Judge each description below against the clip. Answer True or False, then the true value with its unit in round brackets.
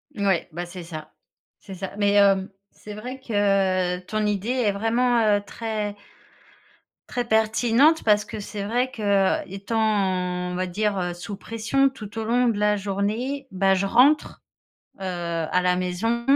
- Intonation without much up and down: False (3.3 semitones)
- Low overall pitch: False (205 Hz)